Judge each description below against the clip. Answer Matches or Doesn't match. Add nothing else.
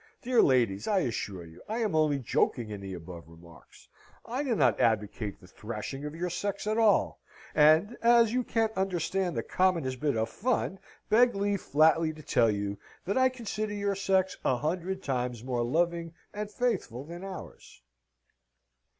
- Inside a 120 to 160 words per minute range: Doesn't match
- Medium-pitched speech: Matches